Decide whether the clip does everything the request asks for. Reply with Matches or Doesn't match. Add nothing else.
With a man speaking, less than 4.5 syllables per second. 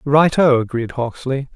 Matches